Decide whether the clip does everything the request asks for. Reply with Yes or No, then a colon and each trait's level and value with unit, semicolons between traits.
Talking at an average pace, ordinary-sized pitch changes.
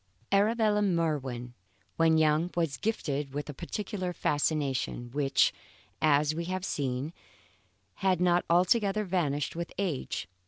No: slow, 120 wpm; average, 4.4 semitones